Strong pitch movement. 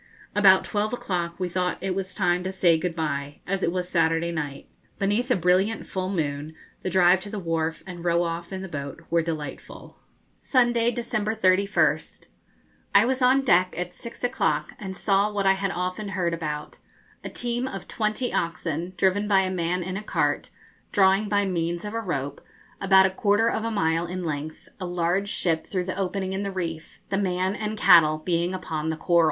No: average, 3.1 semitones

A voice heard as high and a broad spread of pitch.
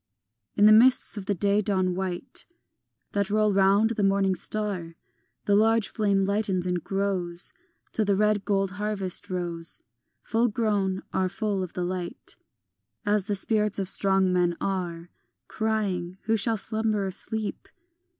No: high, 200 Hz; narrow, 2.4 semitones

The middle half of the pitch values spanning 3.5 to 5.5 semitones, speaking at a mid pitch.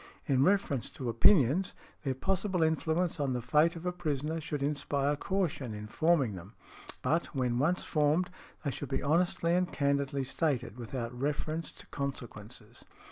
Yes: average, 4.3 semitones; medium, 145 Hz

